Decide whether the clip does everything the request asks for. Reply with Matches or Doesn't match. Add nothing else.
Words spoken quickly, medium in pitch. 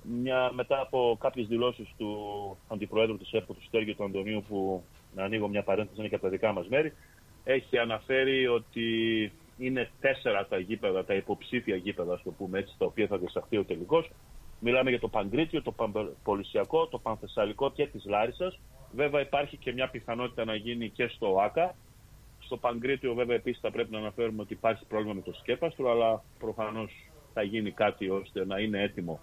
Doesn't match